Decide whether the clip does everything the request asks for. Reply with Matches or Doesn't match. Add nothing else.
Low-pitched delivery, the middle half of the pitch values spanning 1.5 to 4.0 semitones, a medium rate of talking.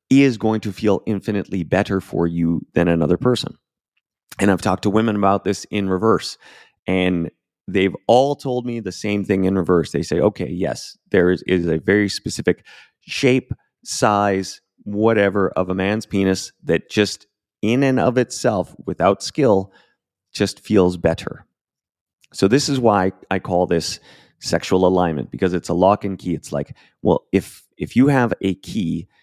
Matches